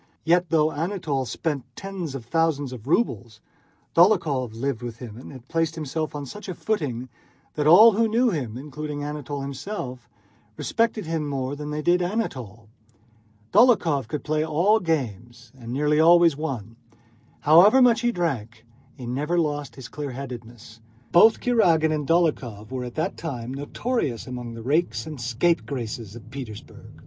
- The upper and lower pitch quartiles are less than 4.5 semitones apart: No, average, 5.3 semitones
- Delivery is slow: No, average, 155 wpm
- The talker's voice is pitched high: No, medium, 145 Hz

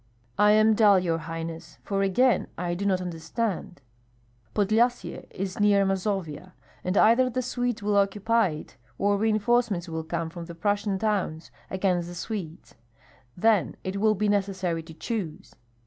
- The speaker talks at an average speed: Yes, average, 150 wpm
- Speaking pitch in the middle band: No, high, 195 Hz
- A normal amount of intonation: Yes, average, 3.7 semitones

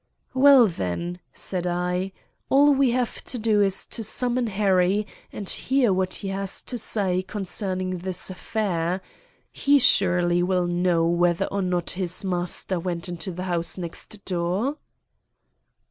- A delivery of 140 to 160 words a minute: Yes, average, 145 wpm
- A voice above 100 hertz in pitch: Yes, medium, 185 Hz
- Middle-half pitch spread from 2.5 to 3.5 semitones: Yes, average, 3.1 semitones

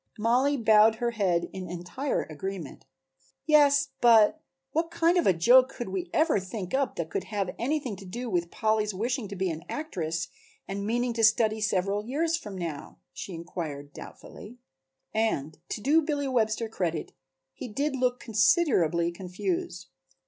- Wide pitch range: Yes, wide, 5.8 semitones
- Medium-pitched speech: No, high, 215 Hz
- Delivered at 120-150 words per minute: No, average, 160 wpm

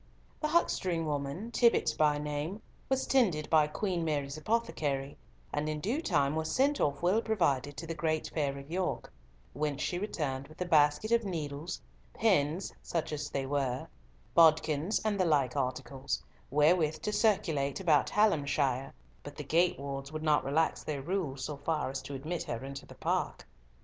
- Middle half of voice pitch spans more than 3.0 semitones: Yes, average, 4.1 semitones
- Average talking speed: Yes, average, 170 wpm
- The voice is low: No, medium, 155 Hz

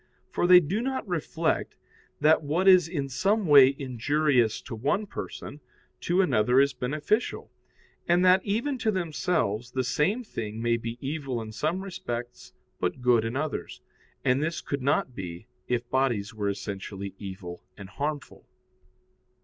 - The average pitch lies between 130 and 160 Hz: Yes, medium, 140 Hz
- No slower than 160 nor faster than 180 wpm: No, average, 150 wpm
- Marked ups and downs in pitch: Yes, wide, 7.1 semitones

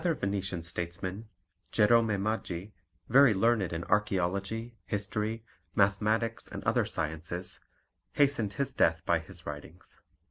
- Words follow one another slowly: Yes, slow, 115 wpm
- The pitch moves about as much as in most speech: Yes, average, 4.3 semitones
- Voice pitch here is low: Yes, low, 100 Hz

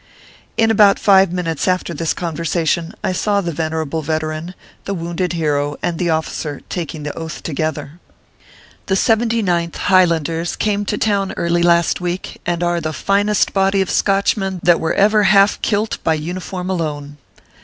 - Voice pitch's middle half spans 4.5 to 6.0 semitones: No, average, 3.4 semitones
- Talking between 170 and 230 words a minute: No, average, 160 wpm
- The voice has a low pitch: No, medium, 175 Hz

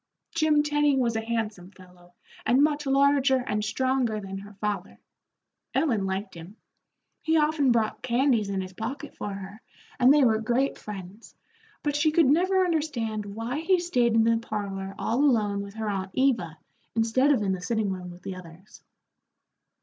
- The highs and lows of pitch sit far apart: Yes, wide, 5.7 semitones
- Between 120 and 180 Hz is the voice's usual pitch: No, high, 225 Hz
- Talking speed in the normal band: Yes, average, 170 wpm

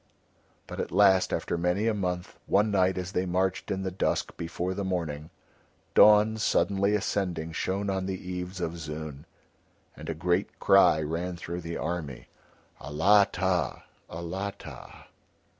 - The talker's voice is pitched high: No, very low, 90 Hz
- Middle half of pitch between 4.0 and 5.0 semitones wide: No, narrow, 2.6 semitones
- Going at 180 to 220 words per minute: No, average, 140 wpm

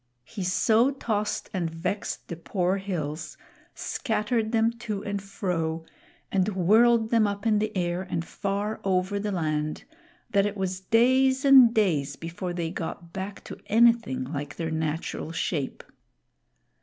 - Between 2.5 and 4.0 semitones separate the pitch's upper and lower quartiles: No, average, 4.5 semitones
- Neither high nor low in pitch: No, high, 195 Hz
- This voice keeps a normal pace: Yes, average, 145 wpm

